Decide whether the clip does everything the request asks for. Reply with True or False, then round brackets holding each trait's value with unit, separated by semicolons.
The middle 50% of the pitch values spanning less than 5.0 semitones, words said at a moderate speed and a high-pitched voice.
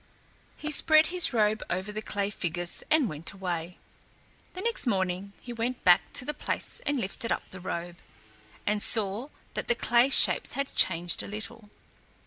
False (5.4 semitones; 170 wpm; 210 Hz)